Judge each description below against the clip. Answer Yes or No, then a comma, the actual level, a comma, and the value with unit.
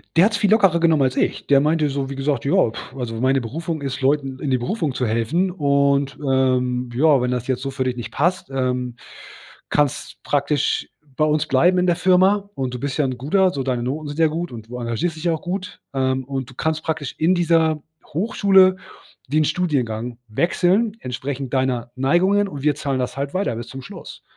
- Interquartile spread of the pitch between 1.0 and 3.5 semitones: No, average, 4.4 semitones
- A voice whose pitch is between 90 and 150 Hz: Yes, medium, 140 Hz